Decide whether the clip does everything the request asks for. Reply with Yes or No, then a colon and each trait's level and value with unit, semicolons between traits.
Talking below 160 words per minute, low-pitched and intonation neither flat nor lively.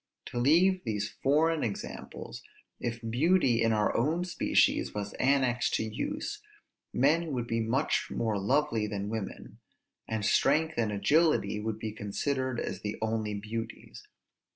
No: average, 140 wpm; low, 115 Hz; wide, 5.7 semitones